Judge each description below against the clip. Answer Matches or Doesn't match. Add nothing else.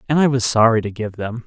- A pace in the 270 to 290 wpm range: Matches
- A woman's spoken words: Doesn't match